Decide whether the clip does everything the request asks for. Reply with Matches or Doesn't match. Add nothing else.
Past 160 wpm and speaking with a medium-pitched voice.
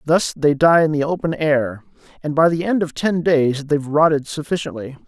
Matches